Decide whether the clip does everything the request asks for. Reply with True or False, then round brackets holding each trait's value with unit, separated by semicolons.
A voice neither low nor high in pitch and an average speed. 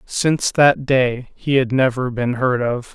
False (130 Hz; 185 wpm)